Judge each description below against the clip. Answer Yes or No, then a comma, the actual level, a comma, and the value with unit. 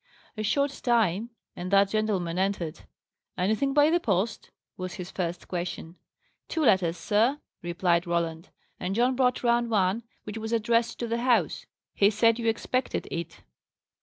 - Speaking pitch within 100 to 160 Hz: No, high, 210 Hz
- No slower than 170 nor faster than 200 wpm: No, average, 155 wpm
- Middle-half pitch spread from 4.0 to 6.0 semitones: Yes, average, 4.8 semitones